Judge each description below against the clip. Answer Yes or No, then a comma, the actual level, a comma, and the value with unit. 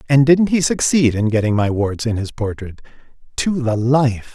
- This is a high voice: No, low, 125 Hz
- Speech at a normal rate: Yes, average, 180 wpm